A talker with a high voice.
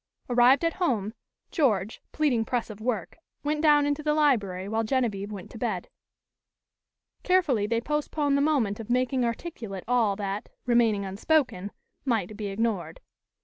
Yes: high, 235 Hz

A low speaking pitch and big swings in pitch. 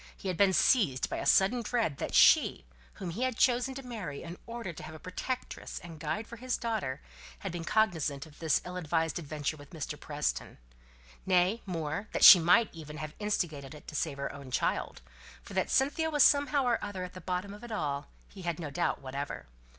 No: medium, 180 Hz; wide, 6.5 semitones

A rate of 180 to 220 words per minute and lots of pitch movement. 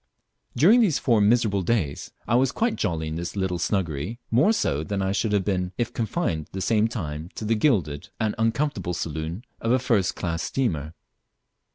Yes: average, 185 wpm; wide, 5.9 semitones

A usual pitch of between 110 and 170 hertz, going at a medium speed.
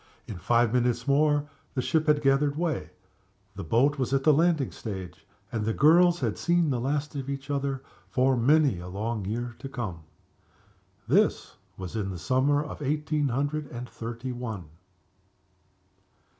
Yes: low, 135 Hz; average, 160 wpm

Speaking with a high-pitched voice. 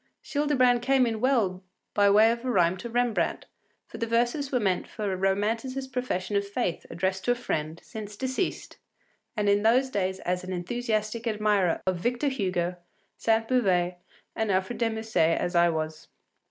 Yes: high, 215 Hz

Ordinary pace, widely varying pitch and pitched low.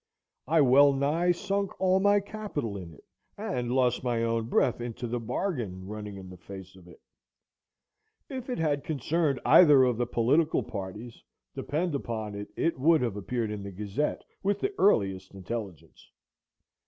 Yes: average, 165 wpm; wide, 7.5 semitones; low, 125 Hz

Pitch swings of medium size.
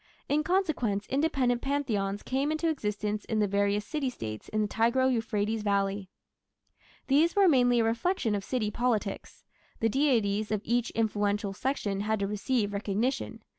Yes: average, 4.5 semitones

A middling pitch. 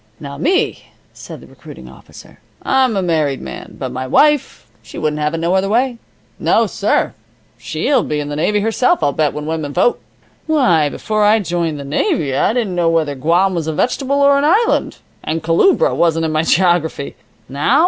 Yes: medium, 170 Hz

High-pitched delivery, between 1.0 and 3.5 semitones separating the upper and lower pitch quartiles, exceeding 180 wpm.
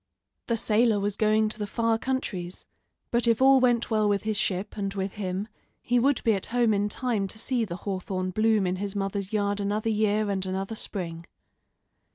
Yes: high, 210 Hz; narrow, 2.5 semitones; average, 200 wpm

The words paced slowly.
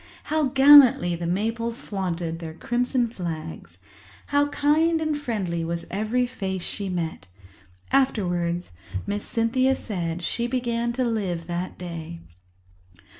Yes: slow, 125 wpm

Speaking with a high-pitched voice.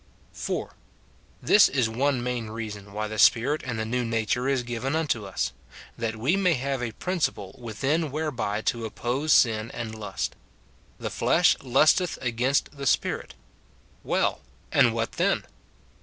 No: low, 120 Hz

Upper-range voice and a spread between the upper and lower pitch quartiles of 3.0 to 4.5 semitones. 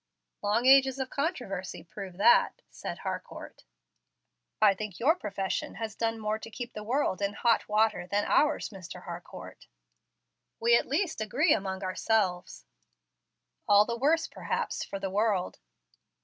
Yes: high, 215 Hz; average, 4.2 semitones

